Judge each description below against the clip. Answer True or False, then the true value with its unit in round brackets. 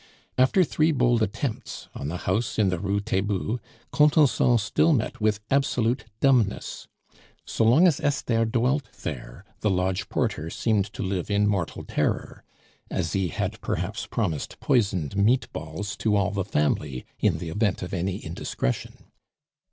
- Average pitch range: True (4.7 semitones)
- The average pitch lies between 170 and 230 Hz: False (105 Hz)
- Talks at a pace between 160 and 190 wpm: False (150 wpm)